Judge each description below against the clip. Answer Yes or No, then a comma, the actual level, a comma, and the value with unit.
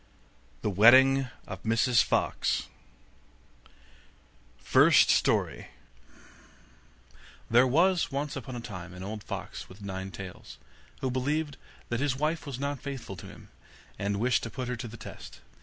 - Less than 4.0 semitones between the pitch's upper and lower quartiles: No, average, 4.7 semitones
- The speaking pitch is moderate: No, low, 125 Hz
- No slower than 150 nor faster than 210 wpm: No, average, 140 wpm